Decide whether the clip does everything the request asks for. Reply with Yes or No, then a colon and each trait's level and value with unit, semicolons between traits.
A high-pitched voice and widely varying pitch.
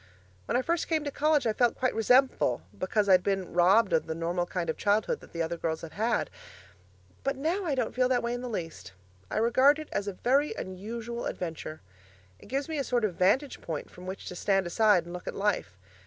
Yes: high, 215 Hz; wide, 6.3 semitones